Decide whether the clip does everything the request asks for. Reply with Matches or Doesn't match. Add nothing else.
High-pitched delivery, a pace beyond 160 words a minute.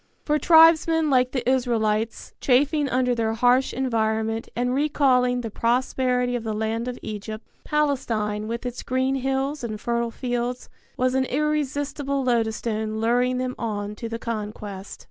Doesn't match